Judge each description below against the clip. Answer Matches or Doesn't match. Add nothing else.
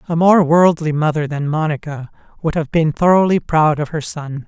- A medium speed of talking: Matches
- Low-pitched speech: Doesn't match